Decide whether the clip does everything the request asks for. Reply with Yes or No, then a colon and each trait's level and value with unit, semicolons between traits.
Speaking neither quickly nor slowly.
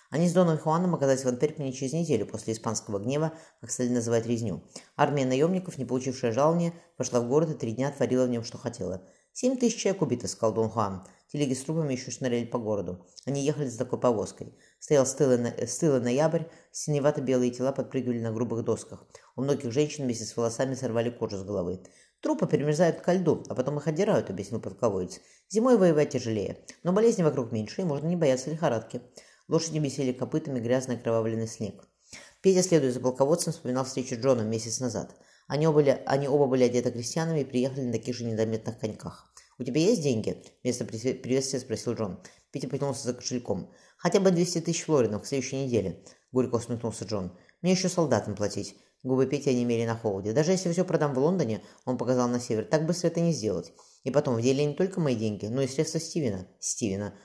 No: fast, 190 wpm